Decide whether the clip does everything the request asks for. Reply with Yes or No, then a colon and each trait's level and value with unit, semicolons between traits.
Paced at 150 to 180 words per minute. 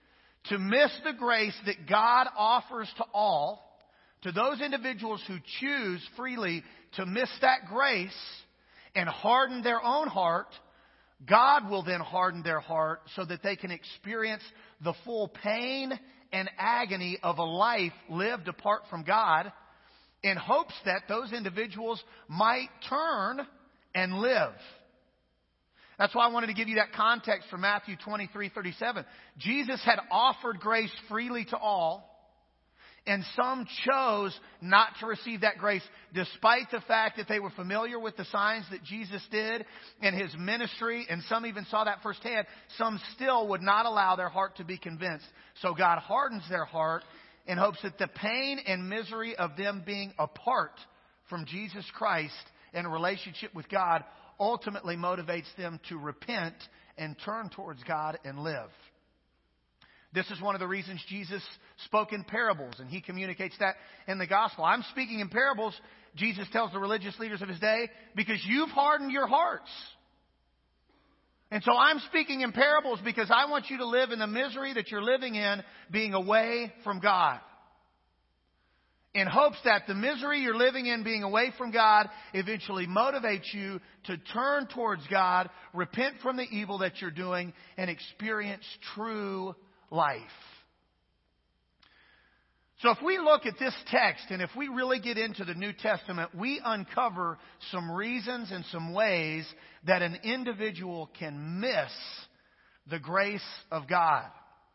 Yes: average, 155 wpm